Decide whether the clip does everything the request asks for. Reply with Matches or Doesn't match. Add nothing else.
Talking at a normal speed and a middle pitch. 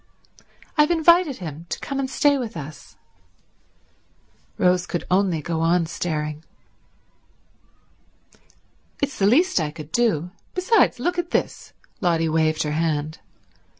Doesn't match